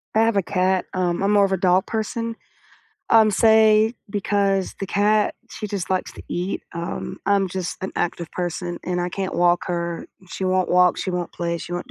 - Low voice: No, high, 190 Hz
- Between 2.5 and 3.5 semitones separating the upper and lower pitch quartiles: Yes, average, 2.8 semitones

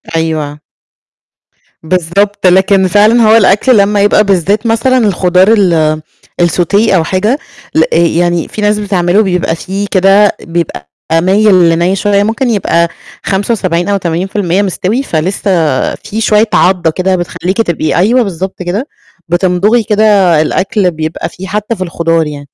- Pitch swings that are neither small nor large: Yes, average, 3.4 semitones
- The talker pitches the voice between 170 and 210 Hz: Yes, high, 190 Hz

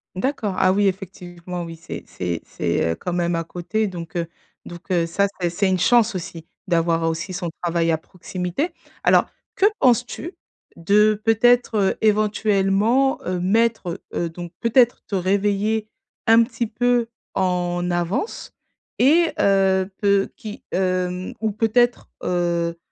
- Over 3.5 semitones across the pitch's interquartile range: Yes, average, 4.0 semitones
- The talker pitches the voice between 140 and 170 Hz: No, high, 190 Hz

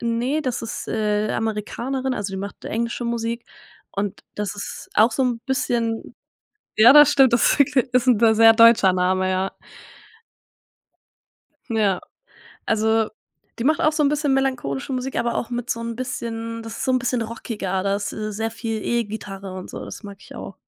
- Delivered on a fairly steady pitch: No, average, 3.3 semitones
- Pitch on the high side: Yes, high, 230 Hz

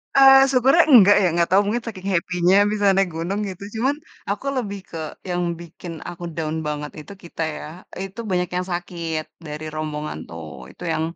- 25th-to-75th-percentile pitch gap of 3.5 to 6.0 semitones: Yes, average, 3.9 semitones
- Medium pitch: Yes, medium, 180 Hz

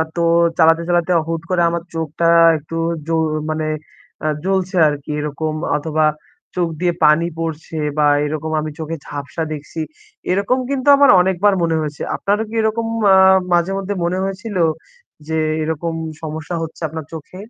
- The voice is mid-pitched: Yes, medium, 165 Hz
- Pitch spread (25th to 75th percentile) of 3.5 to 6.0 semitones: No, average, 3.0 semitones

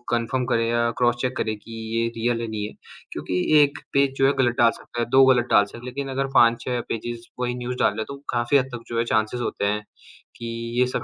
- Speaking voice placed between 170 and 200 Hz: No, low, 120 Hz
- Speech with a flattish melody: Yes, narrow, 1.7 semitones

